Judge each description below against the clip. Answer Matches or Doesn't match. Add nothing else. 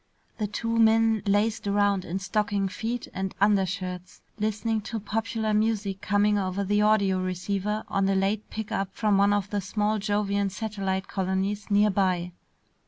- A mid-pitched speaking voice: Doesn't match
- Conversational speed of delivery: Matches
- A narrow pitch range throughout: Matches